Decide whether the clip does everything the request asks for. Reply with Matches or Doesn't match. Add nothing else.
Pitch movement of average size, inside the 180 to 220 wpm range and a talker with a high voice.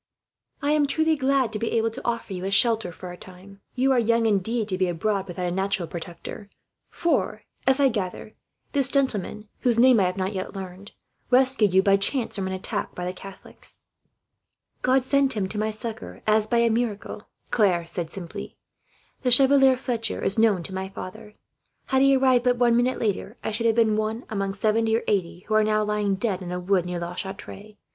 Matches